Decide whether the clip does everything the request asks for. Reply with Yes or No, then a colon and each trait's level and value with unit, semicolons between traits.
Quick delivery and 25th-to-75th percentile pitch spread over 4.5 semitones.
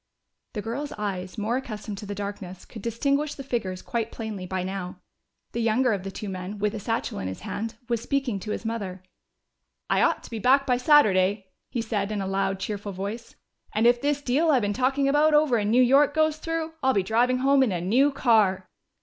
Yes: fast, 220 wpm; average, 5.0 semitones